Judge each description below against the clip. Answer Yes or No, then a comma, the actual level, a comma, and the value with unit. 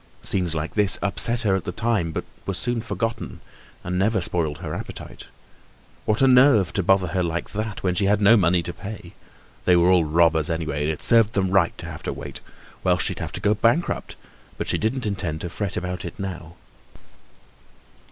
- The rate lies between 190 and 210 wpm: Yes, average, 200 wpm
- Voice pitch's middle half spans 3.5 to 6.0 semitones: Yes, average, 3.9 semitones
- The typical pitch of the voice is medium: No, very low, 95 Hz